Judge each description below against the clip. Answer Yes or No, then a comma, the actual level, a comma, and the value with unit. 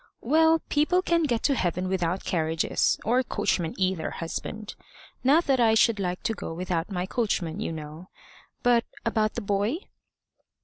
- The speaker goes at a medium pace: Yes, average, 160 wpm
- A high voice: Yes, high, 205 Hz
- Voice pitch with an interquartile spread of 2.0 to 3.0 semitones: No, wide, 5.5 semitones